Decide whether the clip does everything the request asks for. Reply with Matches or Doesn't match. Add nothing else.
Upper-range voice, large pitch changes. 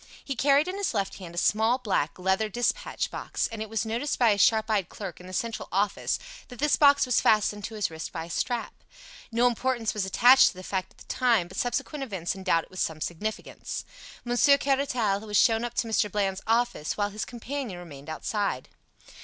Doesn't match